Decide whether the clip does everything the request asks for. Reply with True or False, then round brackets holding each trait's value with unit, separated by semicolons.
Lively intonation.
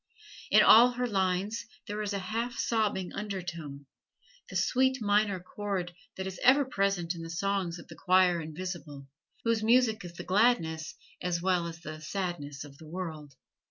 False (4.1 semitones)